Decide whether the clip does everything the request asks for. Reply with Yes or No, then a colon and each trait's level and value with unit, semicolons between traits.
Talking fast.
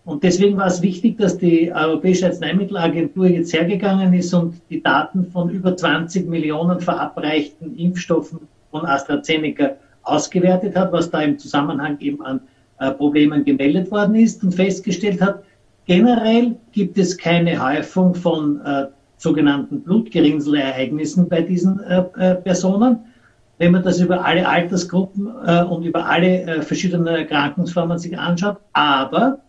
No: average, 140 wpm